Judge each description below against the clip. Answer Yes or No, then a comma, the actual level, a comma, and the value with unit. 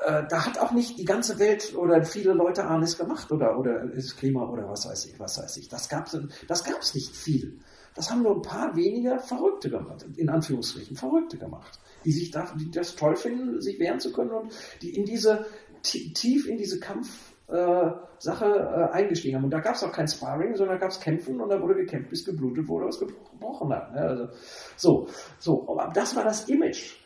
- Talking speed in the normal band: No, fast, 210 wpm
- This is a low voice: No, medium, 185 Hz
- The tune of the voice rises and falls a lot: Yes, wide, 5.9 semitones